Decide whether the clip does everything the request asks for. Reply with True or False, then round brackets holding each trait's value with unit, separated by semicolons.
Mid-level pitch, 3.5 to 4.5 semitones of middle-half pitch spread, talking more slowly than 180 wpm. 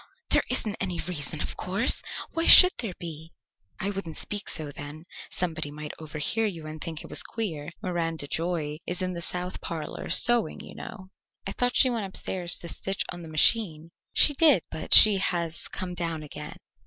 False (175 Hz; 3.8 semitones; 185 wpm)